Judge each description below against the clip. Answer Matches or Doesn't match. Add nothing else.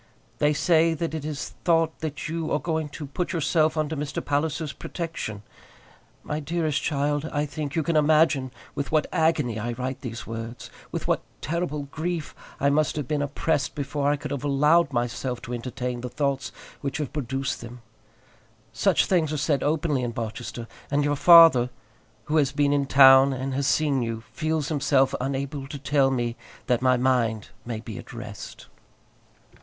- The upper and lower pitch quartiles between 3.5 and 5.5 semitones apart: Doesn't match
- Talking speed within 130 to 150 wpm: Doesn't match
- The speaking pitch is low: Doesn't match